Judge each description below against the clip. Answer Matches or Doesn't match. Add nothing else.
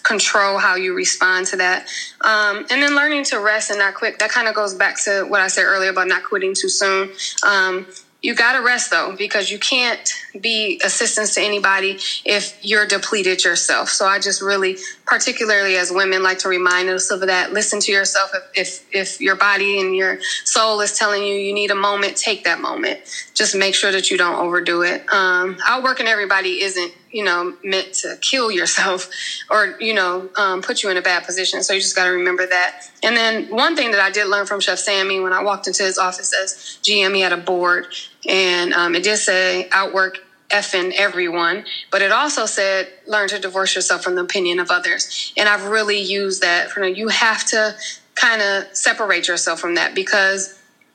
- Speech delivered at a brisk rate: Matches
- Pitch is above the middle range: Matches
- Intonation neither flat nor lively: Doesn't match